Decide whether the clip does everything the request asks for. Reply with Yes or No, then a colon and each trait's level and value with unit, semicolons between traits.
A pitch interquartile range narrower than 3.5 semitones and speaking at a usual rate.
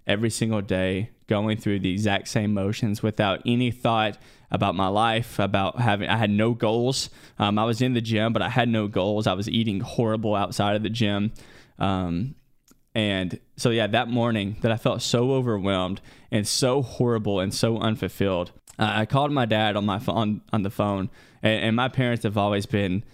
Yes: narrow, 2.6 semitones; average, 190 wpm